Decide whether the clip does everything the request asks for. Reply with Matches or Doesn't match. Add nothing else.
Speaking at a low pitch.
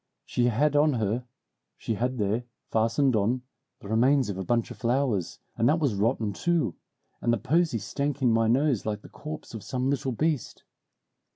Matches